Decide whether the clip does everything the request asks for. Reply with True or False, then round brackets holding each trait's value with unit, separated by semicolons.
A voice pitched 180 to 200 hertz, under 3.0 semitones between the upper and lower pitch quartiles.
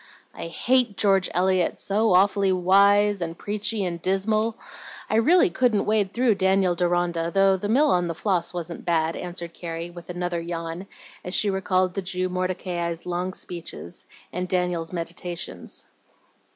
True (185 Hz; 2.5 semitones)